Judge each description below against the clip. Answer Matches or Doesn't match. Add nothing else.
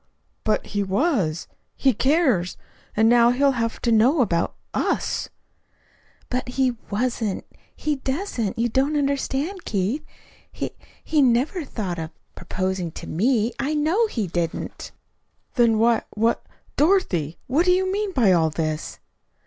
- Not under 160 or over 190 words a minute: Doesn't match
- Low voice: Doesn't match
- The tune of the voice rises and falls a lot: Matches